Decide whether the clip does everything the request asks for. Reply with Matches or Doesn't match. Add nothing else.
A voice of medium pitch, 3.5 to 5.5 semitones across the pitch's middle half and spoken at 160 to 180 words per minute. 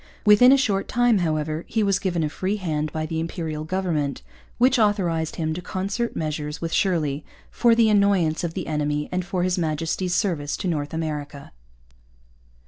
Matches